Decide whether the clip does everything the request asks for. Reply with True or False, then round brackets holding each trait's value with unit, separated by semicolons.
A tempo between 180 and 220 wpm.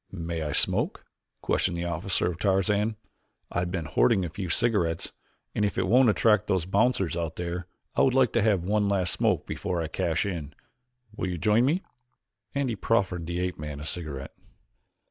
True (190 wpm)